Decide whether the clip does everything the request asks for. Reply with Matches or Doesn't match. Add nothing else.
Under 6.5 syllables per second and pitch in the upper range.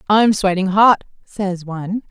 Matches